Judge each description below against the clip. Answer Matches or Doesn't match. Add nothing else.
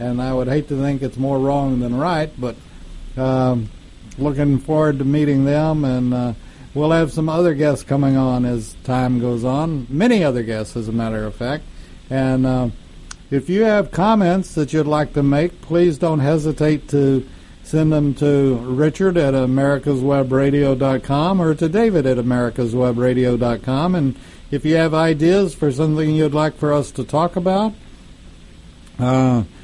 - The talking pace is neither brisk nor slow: Matches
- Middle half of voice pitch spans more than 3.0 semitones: Matches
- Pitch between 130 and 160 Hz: Matches